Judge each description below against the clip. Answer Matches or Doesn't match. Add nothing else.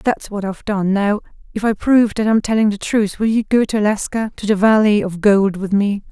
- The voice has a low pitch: Doesn't match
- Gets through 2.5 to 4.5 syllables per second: Doesn't match